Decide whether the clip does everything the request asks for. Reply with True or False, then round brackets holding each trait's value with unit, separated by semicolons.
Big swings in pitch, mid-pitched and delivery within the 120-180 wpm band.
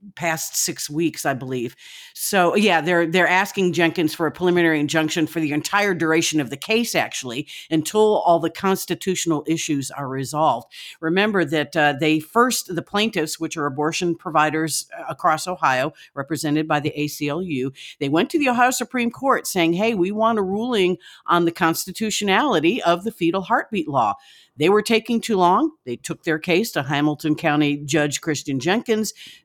False (4.6 semitones; 165 Hz; 170 wpm)